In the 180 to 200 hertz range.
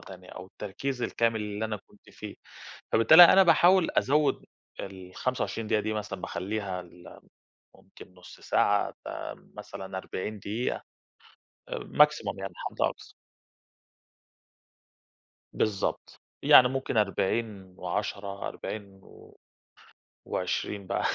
No: low, 105 Hz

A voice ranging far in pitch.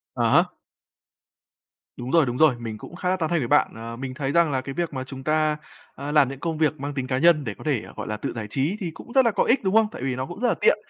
No: average, 4.7 semitones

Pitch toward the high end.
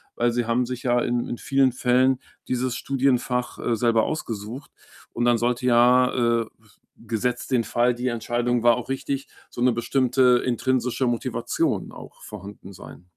No: low, 120 Hz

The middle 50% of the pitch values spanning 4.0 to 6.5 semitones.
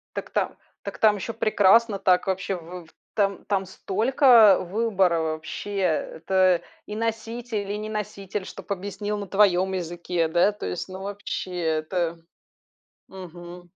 No: average, 2.9 semitones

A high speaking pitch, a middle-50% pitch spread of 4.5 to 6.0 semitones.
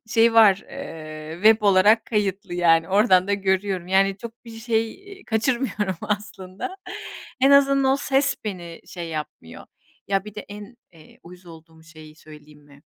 Yes: high, 195 Hz; average, 5.0 semitones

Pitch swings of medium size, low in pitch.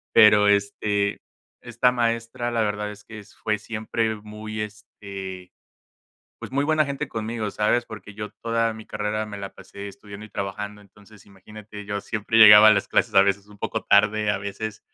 No: narrow, 1.4 semitones; low, 105 Hz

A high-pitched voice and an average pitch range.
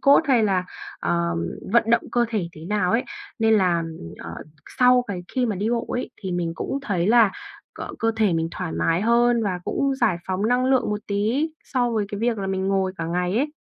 Yes: high, 210 Hz; average, 4.7 semitones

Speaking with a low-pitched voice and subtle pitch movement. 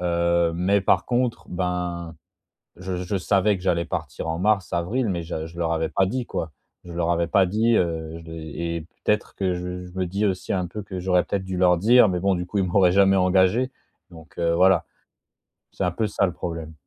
Yes: very low, 90 Hz; narrow, 2.3 semitones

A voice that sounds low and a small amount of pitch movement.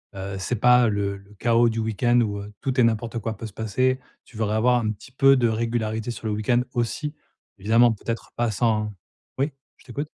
Yes: low, 115 Hz; narrow, 2.3 semitones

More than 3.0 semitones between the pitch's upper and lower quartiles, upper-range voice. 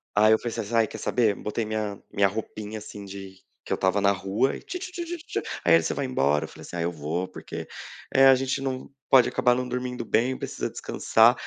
No: average, 4.5 semitones; low, 110 Hz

